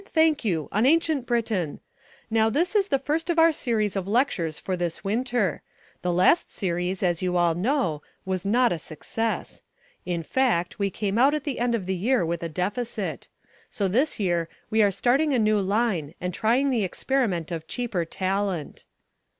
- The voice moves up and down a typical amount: No, wide, 6.0 semitones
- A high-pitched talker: Yes, high, 210 Hz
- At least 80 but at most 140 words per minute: No, average, 185 wpm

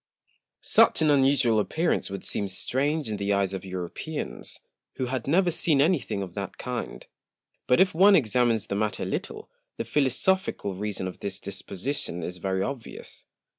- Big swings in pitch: Yes, wide, 6.7 semitones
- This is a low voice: Yes, low, 115 Hz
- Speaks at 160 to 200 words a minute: Yes, average, 170 wpm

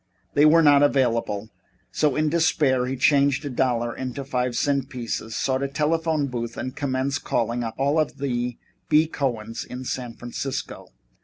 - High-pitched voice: No, low, 130 Hz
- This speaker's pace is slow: No, average, 160 wpm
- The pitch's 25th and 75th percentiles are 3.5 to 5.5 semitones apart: No, average, 3.0 semitones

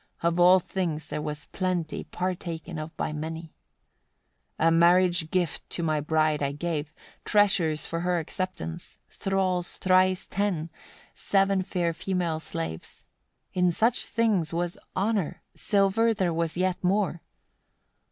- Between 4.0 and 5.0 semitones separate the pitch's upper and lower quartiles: No, average, 2.7 semitones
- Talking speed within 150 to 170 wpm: No, slow, 135 wpm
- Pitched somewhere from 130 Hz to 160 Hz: No, medium, 175 Hz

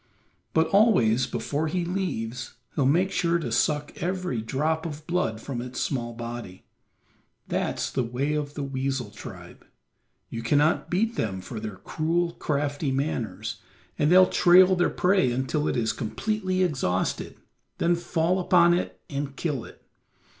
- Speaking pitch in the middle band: Yes, medium, 145 Hz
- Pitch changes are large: Yes, wide, 6.1 semitones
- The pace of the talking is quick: No, average, 150 wpm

